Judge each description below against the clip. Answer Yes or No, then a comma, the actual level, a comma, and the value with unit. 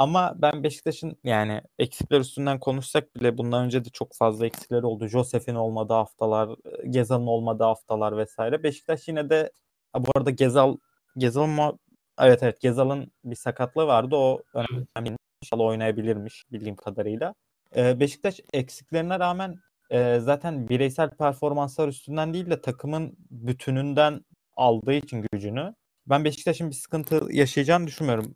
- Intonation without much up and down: No, average, 4.2 semitones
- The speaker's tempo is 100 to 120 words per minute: No, average, 130 wpm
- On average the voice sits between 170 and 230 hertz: No, low, 135 Hz